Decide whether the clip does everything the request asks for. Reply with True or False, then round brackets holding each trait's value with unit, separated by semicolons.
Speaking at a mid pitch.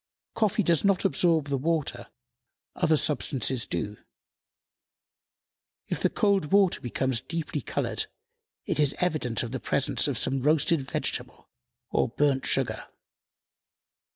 True (145 Hz)